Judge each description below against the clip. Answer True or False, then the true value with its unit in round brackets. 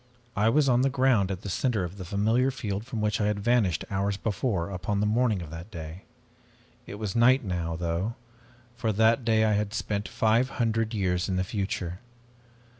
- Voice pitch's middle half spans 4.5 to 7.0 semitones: False (3.6 semitones)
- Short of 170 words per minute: False (195 wpm)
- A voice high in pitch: False (105 Hz)